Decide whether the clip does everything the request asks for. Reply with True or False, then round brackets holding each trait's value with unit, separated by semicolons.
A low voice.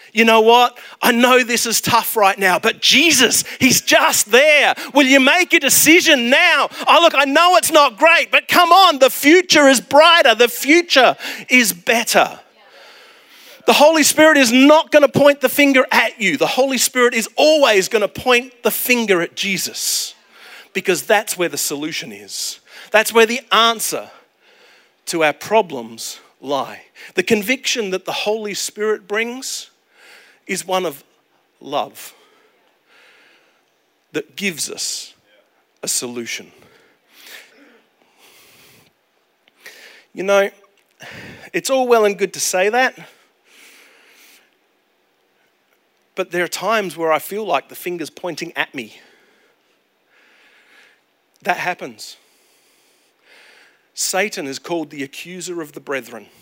False (235 Hz)